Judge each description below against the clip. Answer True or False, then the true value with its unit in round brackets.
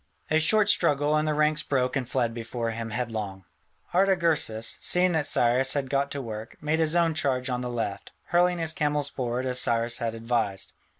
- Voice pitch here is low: True (130 Hz)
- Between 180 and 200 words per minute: True (190 wpm)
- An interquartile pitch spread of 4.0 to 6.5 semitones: True (4.8 semitones)